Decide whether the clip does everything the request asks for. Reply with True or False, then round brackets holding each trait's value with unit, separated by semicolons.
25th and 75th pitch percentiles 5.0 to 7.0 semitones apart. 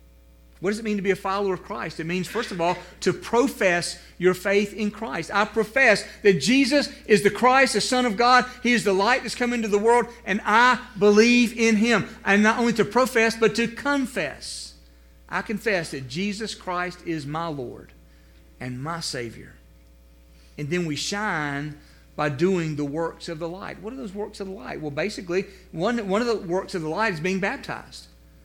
True (5.5 semitones)